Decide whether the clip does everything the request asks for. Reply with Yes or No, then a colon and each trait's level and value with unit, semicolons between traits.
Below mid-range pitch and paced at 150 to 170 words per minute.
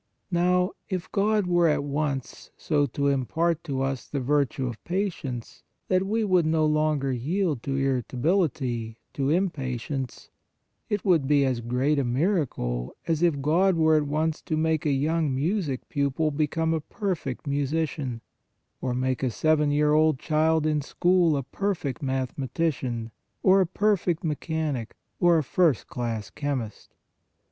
No: medium, 150 Hz; average, 155 wpm